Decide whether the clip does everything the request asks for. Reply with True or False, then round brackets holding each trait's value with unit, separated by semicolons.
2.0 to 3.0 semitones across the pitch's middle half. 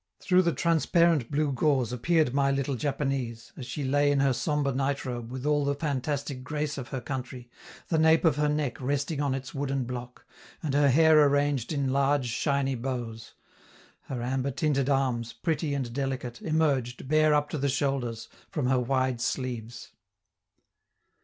True (2.6 semitones)